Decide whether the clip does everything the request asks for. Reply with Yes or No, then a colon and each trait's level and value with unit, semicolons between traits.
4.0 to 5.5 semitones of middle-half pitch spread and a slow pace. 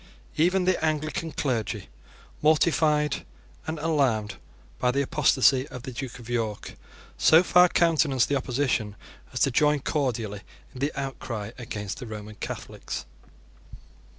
Yes: average, 4.7 semitones; slow, 130 wpm